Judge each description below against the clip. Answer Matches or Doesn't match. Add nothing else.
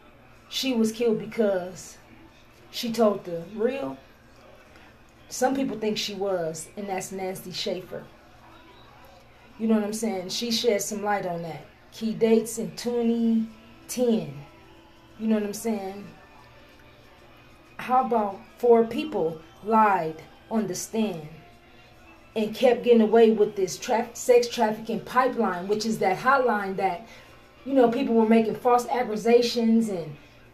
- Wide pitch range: Doesn't match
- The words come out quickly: Doesn't match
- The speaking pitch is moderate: Doesn't match